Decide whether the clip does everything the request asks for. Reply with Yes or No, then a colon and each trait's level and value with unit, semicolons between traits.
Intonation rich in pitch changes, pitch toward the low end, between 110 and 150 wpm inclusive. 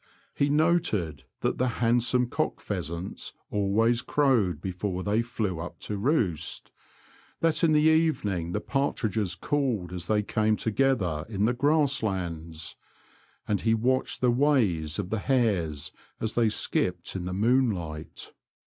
Yes: wide, 6.1 semitones; low, 110 Hz; average, 145 wpm